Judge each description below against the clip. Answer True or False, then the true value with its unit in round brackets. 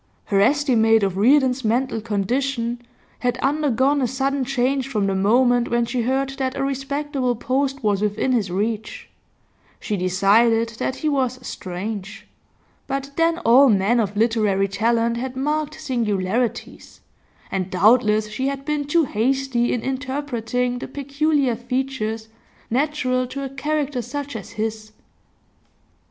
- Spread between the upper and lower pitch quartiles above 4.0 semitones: False (3.7 semitones)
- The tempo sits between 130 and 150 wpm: True (140 wpm)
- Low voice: False (245 Hz)